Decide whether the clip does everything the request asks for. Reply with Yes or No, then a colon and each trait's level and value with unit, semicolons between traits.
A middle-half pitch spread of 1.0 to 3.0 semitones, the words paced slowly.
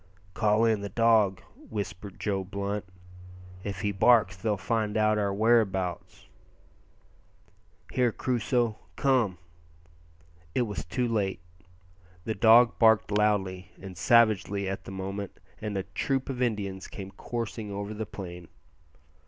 Yes: average, 2.7 semitones; slow, 130 wpm